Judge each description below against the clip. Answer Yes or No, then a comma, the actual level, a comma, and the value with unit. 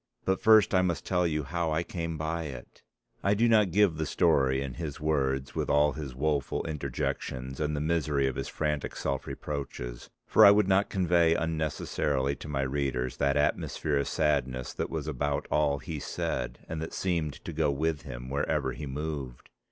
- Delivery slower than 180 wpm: No, average, 190 wpm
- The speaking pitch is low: Yes, very low, 75 Hz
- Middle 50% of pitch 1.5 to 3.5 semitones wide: Yes, average, 3.1 semitones